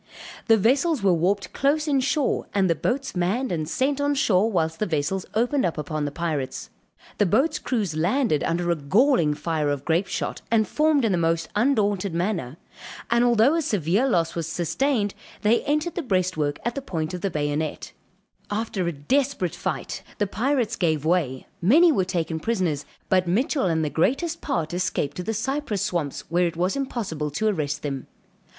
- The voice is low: No, high, 190 Hz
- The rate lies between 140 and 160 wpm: No, average, 185 wpm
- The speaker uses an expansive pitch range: Yes, wide, 7.3 semitones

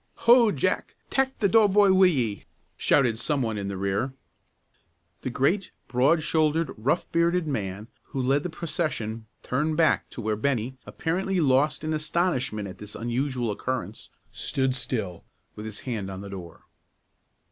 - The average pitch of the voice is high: No, low, 130 Hz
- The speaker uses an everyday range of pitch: No, wide, 7.0 semitones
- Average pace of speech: Yes, average, 160 wpm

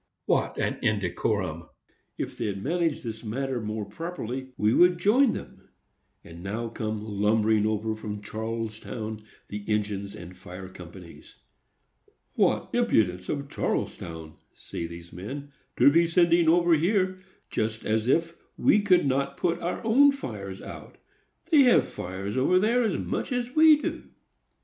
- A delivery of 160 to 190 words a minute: No, average, 140 wpm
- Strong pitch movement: Yes, wide, 9.0 semitones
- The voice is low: Yes, low, 115 Hz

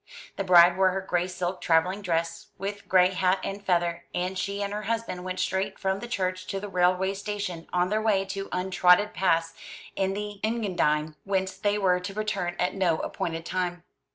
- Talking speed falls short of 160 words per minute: No, average, 190 wpm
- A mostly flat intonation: Yes, narrow, 2.0 semitones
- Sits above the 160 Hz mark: Yes, medium, 185 Hz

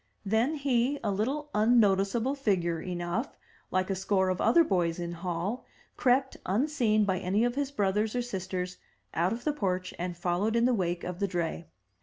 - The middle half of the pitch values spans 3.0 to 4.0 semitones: No, average, 5.1 semitones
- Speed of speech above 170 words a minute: Yes, average, 180 wpm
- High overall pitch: Yes, high, 200 Hz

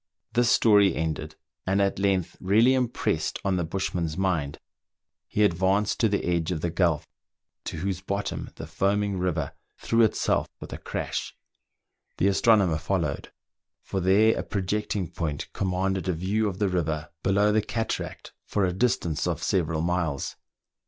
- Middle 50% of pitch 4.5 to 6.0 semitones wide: No, average, 3.3 semitones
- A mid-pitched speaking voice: No, very low, 95 Hz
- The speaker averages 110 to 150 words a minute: No, average, 160 wpm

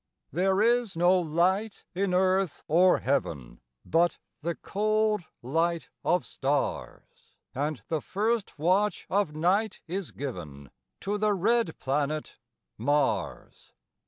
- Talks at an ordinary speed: No, slow, 115 wpm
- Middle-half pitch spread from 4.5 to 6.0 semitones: Yes, average, 5.1 semitones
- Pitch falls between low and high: Yes, medium, 175 Hz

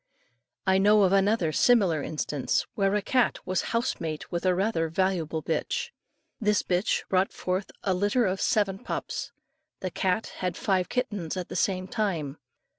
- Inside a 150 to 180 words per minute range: Yes, average, 165 wpm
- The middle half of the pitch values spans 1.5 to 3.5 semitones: Yes, average, 2.8 semitones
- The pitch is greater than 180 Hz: Yes, high, 190 Hz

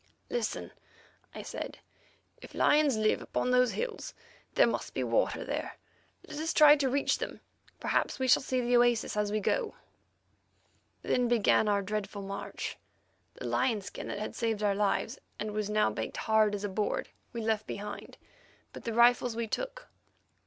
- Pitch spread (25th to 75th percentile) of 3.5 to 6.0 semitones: Yes, average, 3.8 semitones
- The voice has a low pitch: No, high, 225 Hz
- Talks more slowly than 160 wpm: No, average, 170 wpm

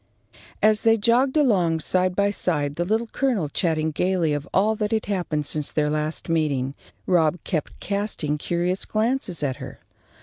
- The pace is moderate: Yes, average, 165 wpm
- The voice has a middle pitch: Yes, medium, 180 Hz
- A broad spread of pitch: Yes, wide, 5.7 semitones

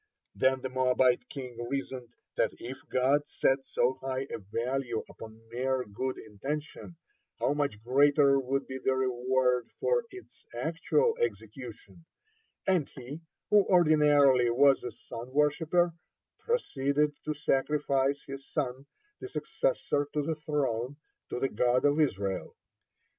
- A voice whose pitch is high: No, low, 135 Hz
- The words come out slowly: Yes, slow, 130 wpm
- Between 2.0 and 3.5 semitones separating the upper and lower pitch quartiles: Yes, average, 2.9 semitones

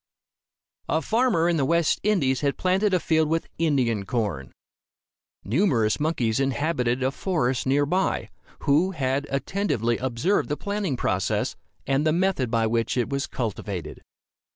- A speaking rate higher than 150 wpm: No, average, 145 wpm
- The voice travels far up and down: Yes, wide, 6.1 semitones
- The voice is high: No, medium, 140 Hz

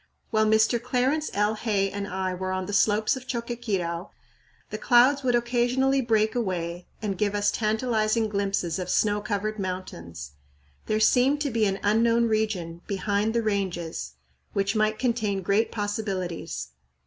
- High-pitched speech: Yes, high, 215 Hz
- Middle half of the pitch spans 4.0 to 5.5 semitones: No, average, 3.3 semitones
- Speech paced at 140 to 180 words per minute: Yes, average, 150 wpm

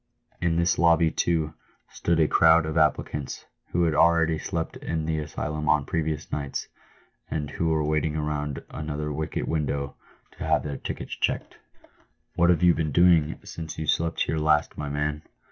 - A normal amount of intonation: No, narrow, 1.6 semitones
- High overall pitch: No, very low, 80 Hz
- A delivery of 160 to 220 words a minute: Yes, average, 175 wpm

